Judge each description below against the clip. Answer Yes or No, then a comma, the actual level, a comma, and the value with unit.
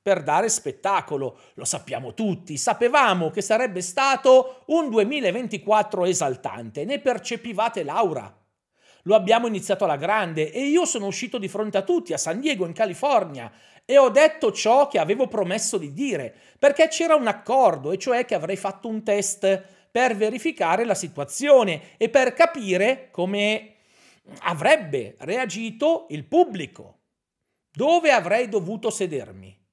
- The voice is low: No, high, 215 Hz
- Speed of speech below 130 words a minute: No, average, 140 wpm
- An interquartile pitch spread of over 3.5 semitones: Yes, average, 5.2 semitones